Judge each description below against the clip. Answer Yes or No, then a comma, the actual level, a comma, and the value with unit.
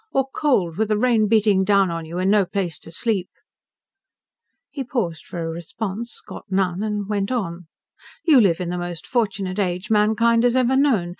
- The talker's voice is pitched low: No, high, 200 Hz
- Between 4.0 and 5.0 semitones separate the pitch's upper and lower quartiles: Yes, average, 4.4 semitones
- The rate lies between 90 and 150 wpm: No, average, 190 wpm